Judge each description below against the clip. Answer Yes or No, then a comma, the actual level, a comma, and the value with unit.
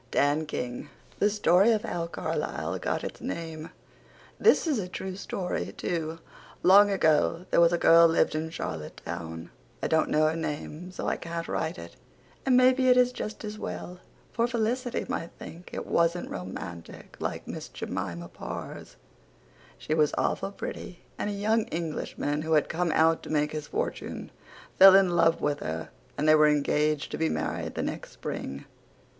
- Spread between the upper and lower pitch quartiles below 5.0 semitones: Yes, average, 4.4 semitones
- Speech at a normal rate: Yes, average, 175 wpm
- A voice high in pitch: No, medium, 165 Hz